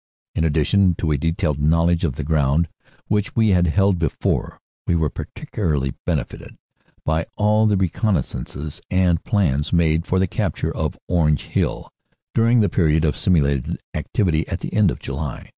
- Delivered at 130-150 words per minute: No, average, 165 wpm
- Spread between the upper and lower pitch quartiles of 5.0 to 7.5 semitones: No, average, 4.0 semitones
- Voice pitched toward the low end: Yes, very low, 85 Hz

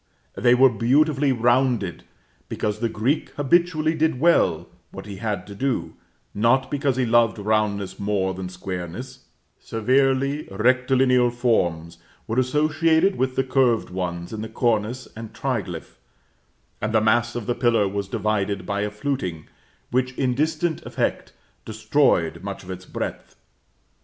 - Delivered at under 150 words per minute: Yes, average, 140 wpm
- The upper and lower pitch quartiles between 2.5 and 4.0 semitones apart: No, average, 4.6 semitones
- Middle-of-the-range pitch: No, low, 120 Hz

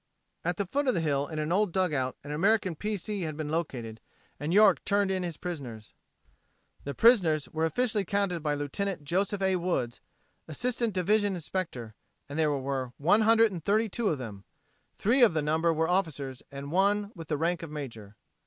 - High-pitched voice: No, medium, 170 Hz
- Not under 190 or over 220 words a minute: No, average, 180 wpm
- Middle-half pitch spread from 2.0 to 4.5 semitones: No, wide, 5.5 semitones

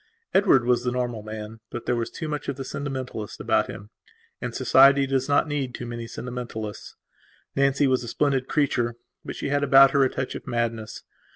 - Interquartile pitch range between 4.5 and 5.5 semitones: No, average, 2.7 semitones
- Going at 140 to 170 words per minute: No, average, 195 wpm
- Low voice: Yes, low, 125 Hz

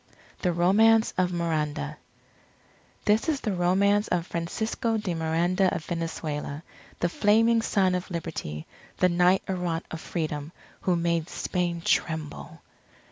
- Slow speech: Yes, slow, 130 wpm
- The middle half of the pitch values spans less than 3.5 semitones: Yes, average, 2.9 semitones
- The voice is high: No, medium, 175 Hz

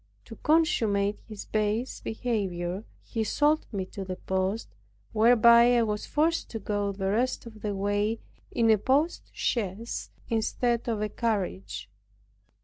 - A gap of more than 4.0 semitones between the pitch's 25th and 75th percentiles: No, average, 2.9 semitones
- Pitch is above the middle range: Yes, high, 220 Hz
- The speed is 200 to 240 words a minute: No, average, 140 wpm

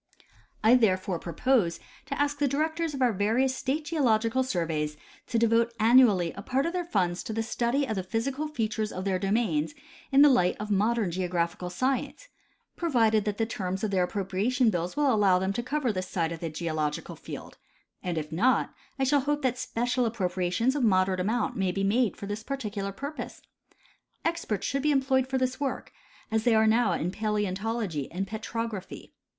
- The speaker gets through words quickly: No, average, 190 wpm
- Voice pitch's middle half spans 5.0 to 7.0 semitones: Yes, wide, 5.6 semitones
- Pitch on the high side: Yes, high, 220 Hz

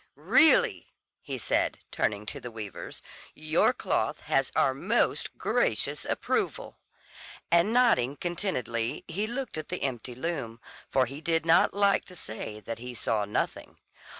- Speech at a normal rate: Yes, average, 145 wpm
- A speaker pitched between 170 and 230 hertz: No, medium, 140 Hz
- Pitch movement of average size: No, wide, 7.9 semitones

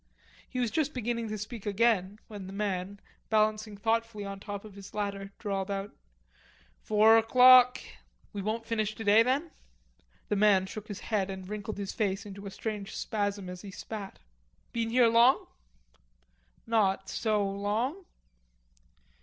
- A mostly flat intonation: Yes, narrow, 2.3 semitones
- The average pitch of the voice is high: Yes, high, 210 Hz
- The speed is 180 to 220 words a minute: No, average, 150 wpm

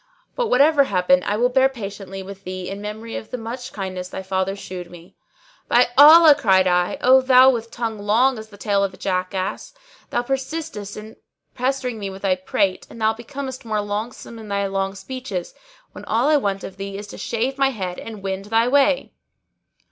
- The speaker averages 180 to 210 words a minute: Yes, average, 200 wpm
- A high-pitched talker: Yes, high, 215 Hz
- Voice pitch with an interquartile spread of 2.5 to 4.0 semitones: No, average, 4.7 semitones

